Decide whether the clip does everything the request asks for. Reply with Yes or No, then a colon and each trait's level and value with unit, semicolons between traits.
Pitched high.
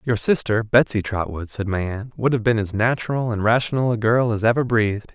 No: low, 110 Hz